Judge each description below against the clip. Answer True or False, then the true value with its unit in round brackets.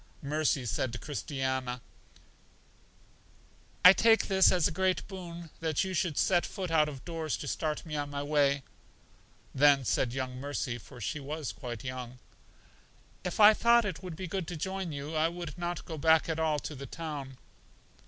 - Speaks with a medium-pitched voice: True (155 Hz)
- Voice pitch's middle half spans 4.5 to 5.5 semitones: False (4.1 semitones)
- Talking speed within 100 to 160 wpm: False (175 wpm)